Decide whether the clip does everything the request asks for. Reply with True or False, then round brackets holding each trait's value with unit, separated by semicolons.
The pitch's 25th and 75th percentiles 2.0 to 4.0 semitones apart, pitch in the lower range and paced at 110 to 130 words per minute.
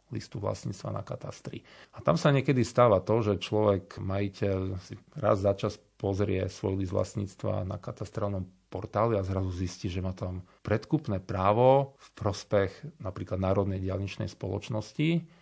False (2.6 semitones; 100 Hz; 150 wpm)